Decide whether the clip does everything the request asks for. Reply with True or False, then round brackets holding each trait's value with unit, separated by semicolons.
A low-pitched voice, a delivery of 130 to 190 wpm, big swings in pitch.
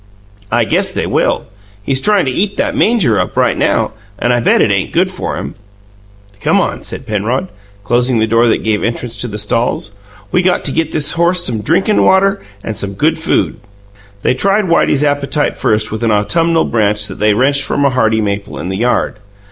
False (125 Hz; 205 wpm; 7.4 semitones)